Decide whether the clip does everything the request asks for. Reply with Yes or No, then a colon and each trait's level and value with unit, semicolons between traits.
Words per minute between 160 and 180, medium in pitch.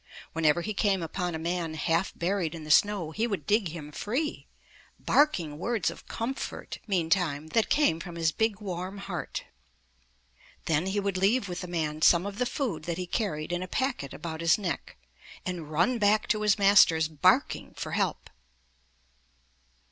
Yes: average, 175 wpm; medium, 180 Hz